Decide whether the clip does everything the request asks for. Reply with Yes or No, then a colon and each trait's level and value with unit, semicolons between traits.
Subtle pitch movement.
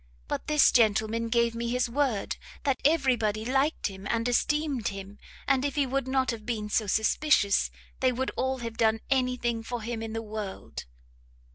No: average, 3.2 semitones